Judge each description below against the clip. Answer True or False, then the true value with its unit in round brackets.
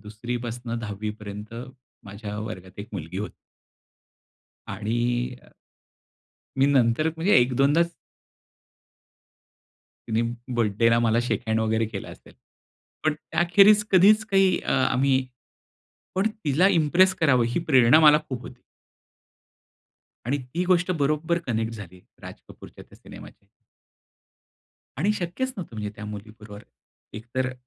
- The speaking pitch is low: True (125 Hz)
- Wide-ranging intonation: True (6.9 semitones)